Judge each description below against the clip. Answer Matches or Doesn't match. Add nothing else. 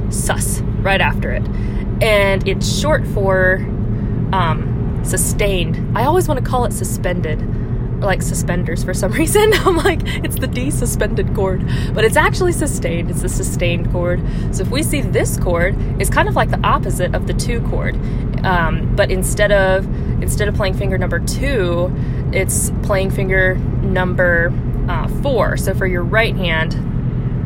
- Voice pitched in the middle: Doesn't match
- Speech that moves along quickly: Doesn't match